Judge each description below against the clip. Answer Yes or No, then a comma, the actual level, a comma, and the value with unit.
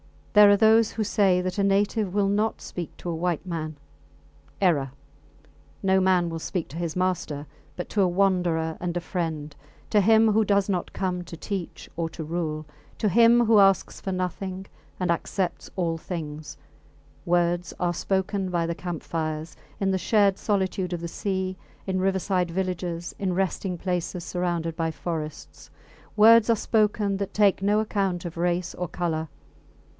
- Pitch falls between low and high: Yes, medium, 180 Hz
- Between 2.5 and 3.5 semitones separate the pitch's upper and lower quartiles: Yes, average, 2.8 semitones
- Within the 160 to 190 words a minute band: Yes, average, 170 wpm